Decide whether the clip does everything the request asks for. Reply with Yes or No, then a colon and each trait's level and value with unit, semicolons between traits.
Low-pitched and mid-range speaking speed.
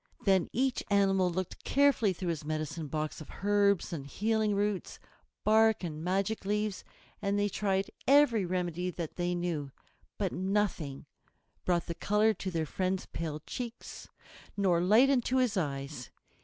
No: high, 190 Hz; average, 150 wpm